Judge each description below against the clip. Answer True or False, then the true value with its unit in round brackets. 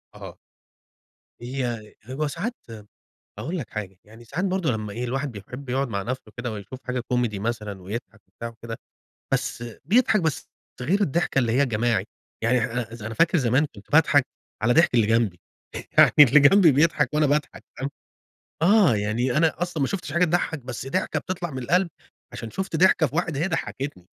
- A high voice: False (130 Hz)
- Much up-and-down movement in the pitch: True (5.9 semitones)